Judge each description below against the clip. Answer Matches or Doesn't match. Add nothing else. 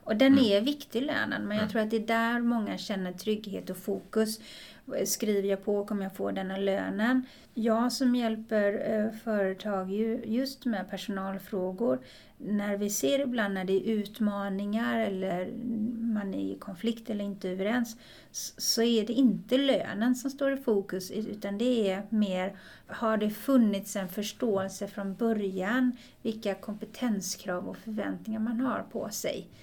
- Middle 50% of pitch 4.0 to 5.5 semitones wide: Doesn't match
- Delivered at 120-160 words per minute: Matches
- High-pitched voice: Matches